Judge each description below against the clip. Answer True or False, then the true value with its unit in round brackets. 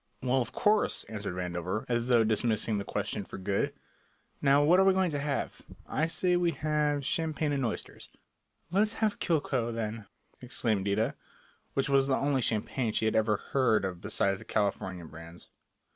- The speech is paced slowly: False (175 wpm)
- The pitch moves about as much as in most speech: False (6.1 semitones)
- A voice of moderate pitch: False (120 Hz)